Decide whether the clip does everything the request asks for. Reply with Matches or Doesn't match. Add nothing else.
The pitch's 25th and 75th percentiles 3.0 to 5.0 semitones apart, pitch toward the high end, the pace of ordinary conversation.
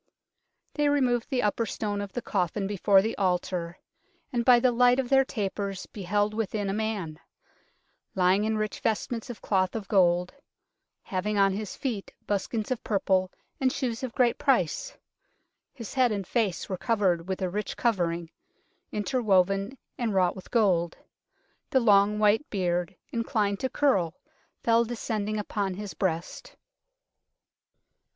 Matches